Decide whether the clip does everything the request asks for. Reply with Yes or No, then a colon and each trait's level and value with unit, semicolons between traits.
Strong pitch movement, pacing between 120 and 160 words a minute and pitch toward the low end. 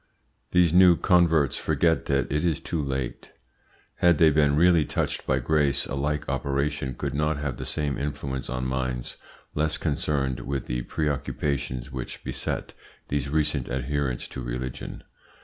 No: narrow, 2.6 semitones; average, 150 wpm; very low, 70 Hz